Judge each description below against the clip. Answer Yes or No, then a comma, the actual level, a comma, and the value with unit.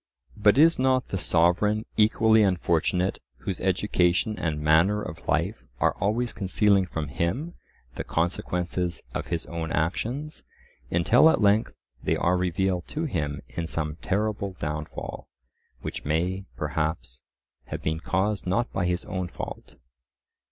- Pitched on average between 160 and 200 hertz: No, very low, 90 Hz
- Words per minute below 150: Yes, slow, 135 wpm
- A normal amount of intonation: Yes, average, 4.2 semitones